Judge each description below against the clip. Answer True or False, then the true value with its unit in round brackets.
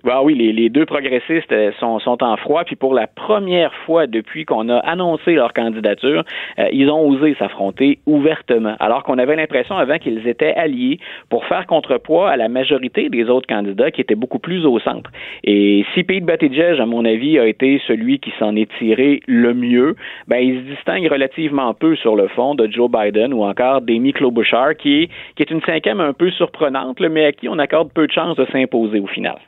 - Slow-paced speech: False (200 wpm)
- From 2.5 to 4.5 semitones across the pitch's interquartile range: False (5.6 semitones)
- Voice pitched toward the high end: False (135 Hz)